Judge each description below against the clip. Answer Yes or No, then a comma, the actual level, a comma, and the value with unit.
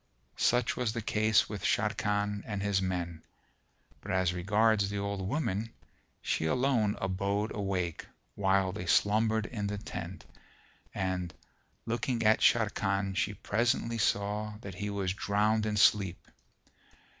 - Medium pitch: No, low, 105 Hz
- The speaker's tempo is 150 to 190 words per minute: No, slow, 135 wpm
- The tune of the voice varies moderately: No, narrow, 2.2 semitones